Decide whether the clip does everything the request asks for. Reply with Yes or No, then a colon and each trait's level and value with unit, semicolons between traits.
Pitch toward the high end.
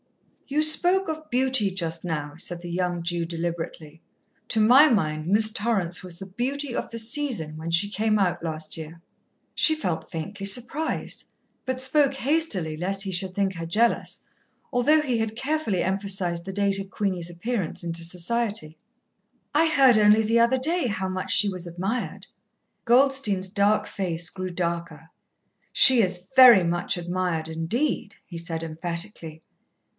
Yes: high, 195 Hz